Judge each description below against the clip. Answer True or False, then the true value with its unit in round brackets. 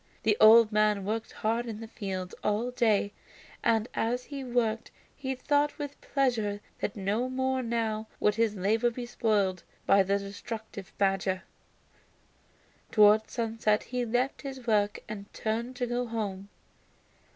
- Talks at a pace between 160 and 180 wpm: False (145 wpm)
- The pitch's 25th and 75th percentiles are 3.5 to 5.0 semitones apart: False (2.8 semitones)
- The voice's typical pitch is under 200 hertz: False (220 Hz)